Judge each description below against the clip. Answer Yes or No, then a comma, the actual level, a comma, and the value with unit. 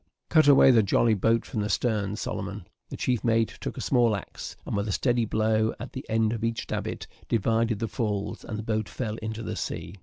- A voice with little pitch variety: Yes, narrow, 1.7 semitones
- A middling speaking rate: No, fast, 220 wpm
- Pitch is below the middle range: Yes, low, 110 Hz